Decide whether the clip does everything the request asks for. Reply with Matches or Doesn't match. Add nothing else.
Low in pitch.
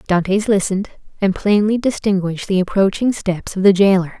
Doesn't match